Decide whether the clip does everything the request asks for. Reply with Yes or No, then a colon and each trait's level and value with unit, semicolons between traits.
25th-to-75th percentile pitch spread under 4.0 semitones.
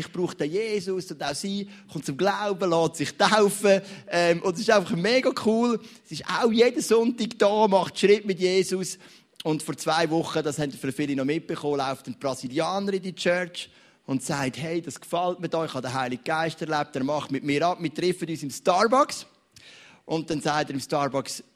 No: average, 4.9 semitones